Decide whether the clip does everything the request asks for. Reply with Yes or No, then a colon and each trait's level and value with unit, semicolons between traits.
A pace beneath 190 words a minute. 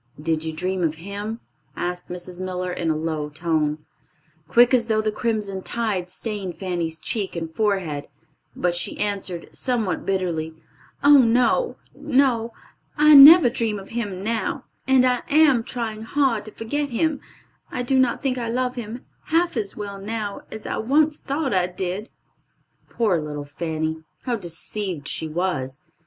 Yes: average, 160 wpm